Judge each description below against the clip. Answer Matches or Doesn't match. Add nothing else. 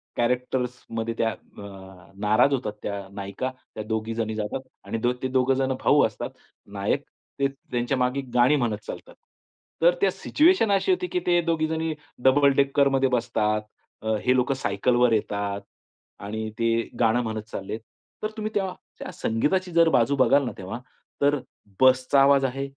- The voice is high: Doesn't match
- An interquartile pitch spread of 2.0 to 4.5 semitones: Matches